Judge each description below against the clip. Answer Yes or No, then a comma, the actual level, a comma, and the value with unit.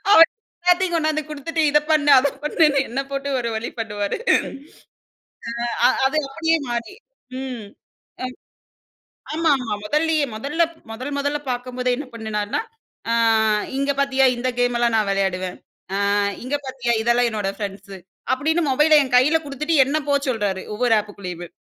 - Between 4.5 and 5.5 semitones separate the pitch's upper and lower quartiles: Yes, average, 5.2 semitones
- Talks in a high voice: Yes, very high, 260 Hz